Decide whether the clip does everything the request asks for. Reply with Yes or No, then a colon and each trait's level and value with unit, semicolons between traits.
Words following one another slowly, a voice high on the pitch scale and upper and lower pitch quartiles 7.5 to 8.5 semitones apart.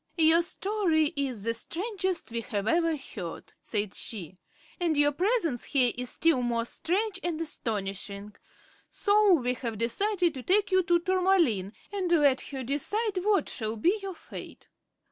No: average, 155 wpm; very high, 315 Hz; wide, 8.1 semitones